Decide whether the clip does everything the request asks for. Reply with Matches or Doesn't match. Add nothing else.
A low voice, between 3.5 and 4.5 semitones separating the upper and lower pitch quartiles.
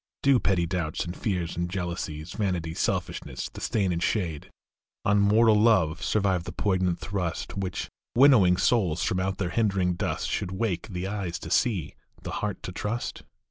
Doesn't match